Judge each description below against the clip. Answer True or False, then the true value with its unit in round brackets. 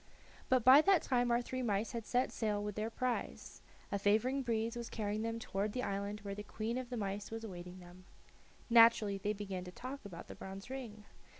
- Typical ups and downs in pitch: True (3.2 semitones)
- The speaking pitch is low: False (215 Hz)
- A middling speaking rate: False (210 wpm)